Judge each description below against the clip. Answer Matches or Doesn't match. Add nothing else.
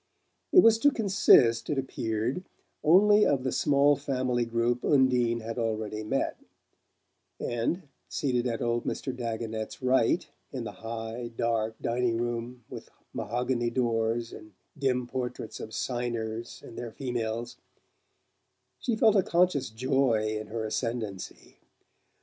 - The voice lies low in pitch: Matches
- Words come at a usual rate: Doesn't match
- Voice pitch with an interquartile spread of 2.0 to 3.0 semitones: Matches